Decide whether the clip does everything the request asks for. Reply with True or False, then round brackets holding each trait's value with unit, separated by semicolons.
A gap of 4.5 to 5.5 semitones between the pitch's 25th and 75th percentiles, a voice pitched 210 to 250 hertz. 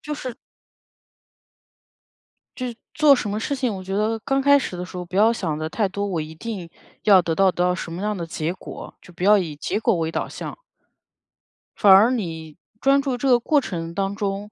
False (4.8 semitones; 200 Hz)